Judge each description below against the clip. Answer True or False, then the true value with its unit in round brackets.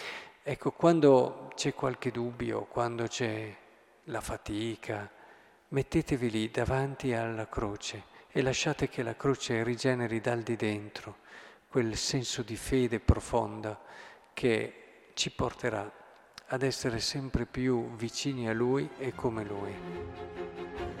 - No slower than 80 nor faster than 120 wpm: True (115 wpm)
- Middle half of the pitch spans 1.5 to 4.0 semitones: True (3.1 semitones)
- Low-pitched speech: True (120 Hz)